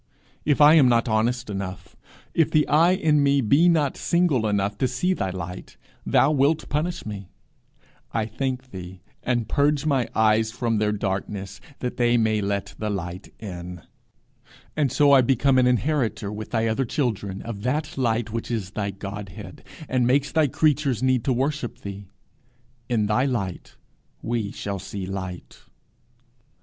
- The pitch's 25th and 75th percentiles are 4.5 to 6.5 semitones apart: Yes, wide, 5.4 semitones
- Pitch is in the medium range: No, low, 115 Hz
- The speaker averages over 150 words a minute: Yes, average, 160 wpm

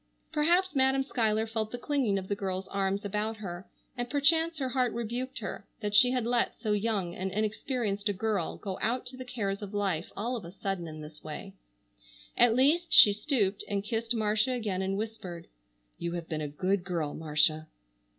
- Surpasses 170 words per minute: Yes, average, 195 wpm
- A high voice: Yes, high, 210 Hz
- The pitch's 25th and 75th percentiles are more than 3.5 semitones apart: Yes, average, 4.4 semitones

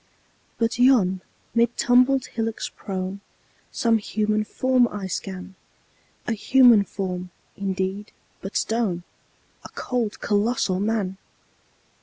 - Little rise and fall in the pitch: No, average, 3.7 semitones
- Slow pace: Yes, slow, 105 wpm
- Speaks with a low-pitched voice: No, high, 215 Hz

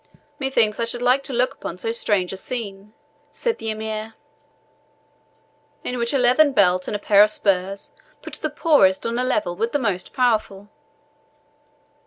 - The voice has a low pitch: No, high, 220 Hz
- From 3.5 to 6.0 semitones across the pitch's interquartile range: Yes, average, 3.9 semitones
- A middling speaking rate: Yes, average, 170 wpm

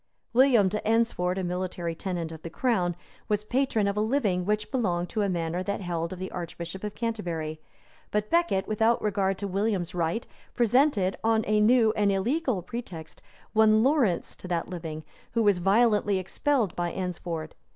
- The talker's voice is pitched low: No, high, 200 Hz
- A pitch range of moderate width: Yes, average, 4.0 semitones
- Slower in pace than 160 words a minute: No, average, 170 wpm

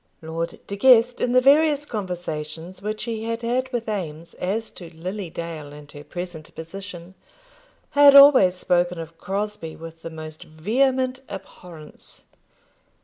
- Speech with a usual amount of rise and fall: No, wide, 6.0 semitones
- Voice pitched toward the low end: No, medium, 185 Hz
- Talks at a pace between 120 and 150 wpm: Yes, average, 145 wpm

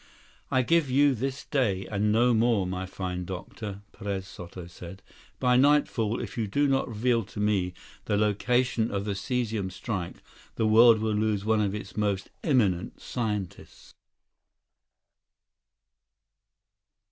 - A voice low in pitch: Yes, low, 105 Hz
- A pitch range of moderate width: Yes, average, 3.9 semitones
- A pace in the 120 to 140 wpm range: Yes, slow, 135 wpm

